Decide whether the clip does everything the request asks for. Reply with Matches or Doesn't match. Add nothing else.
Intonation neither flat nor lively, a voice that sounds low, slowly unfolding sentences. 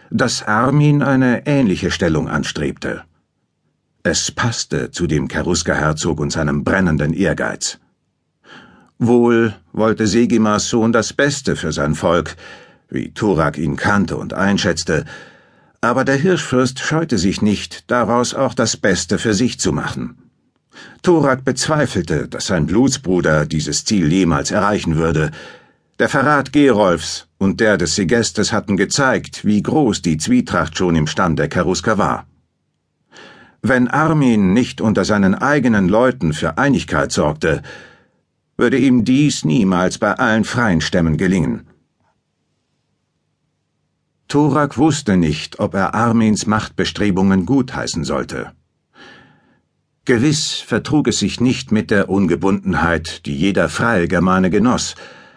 Doesn't match